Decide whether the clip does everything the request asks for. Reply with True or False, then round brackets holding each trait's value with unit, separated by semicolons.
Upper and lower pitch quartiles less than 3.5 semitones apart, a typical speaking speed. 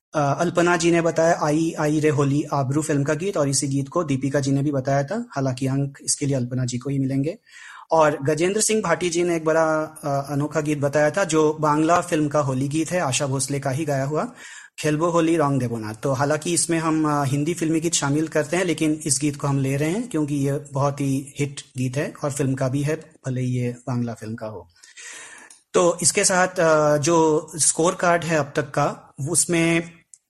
False (2.8 semitones; 215 wpm)